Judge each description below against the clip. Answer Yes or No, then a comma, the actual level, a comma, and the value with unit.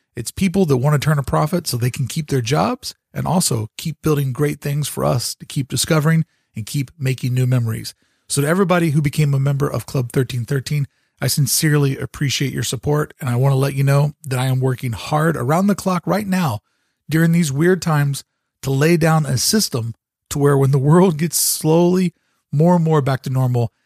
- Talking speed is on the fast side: Yes, fast, 210 wpm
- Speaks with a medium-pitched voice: Yes, medium, 145 Hz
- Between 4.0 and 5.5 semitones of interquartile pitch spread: No, average, 3.4 semitones